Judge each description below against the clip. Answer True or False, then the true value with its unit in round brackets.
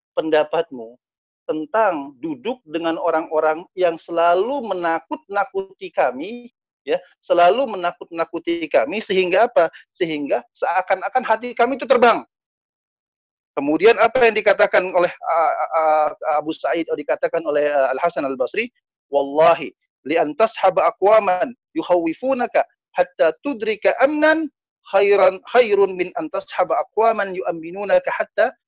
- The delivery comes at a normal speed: True (115 wpm)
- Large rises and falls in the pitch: True (7.6 semitones)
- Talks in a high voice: True (195 Hz)